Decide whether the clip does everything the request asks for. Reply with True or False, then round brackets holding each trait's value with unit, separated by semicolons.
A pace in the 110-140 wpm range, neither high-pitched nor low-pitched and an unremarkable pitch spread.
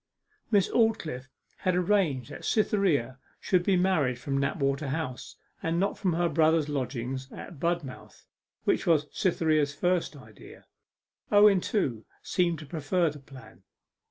True (135 wpm; 160 Hz; 4.9 semitones)